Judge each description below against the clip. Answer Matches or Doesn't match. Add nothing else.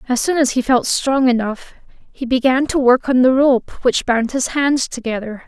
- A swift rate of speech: Matches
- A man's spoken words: Doesn't match